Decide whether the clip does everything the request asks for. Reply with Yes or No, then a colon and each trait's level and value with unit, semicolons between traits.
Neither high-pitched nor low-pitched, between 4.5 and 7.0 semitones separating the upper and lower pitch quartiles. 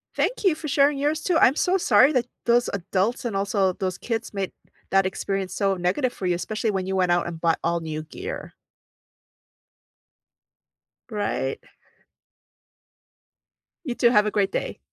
No: high, 205 Hz; average, 5.2 semitones